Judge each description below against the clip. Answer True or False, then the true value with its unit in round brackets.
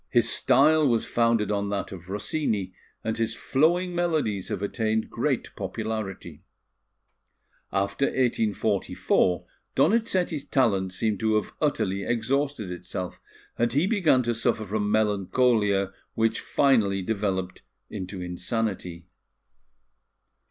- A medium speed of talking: False (110 wpm)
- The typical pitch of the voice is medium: False (110 Hz)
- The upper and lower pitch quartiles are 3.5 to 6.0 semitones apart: True (4.7 semitones)